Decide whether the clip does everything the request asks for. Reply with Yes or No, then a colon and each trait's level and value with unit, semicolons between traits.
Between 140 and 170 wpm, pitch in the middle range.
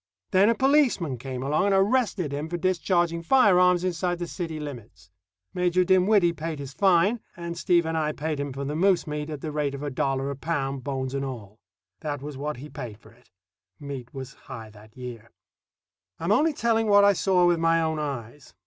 No: fast, 205 wpm; medium, 155 Hz